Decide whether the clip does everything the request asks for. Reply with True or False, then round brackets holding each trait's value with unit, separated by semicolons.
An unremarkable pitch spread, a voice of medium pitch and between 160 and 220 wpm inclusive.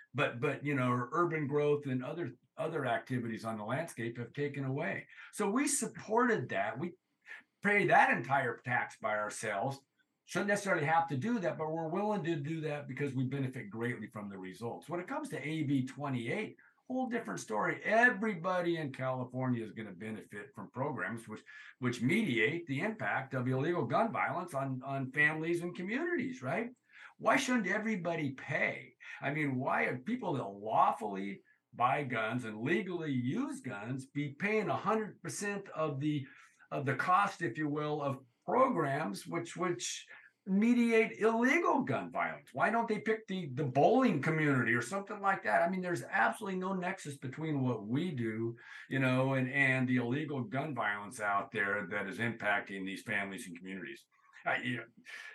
False (7.1 semitones; 145 Hz; 165 wpm)